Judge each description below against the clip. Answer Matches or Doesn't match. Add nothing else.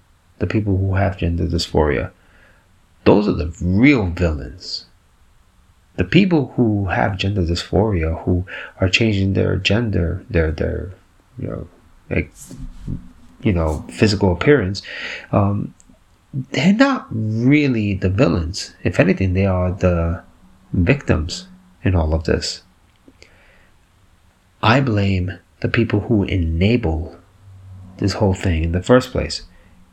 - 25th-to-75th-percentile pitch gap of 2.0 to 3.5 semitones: Matches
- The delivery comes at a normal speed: Doesn't match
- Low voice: Matches